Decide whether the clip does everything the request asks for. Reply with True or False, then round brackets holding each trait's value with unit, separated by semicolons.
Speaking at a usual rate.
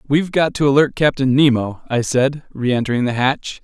True (180 wpm)